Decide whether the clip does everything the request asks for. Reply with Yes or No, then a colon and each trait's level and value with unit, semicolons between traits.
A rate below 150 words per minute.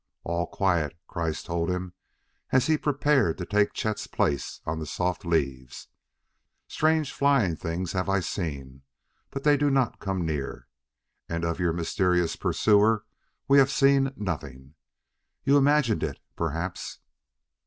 Yes: average, 140 wpm